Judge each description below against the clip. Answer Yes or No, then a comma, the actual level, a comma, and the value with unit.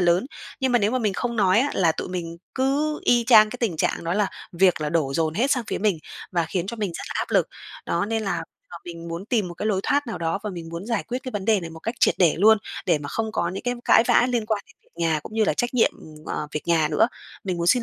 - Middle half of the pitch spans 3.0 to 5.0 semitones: No, wide, 5.4 semitones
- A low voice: No, high, 200 Hz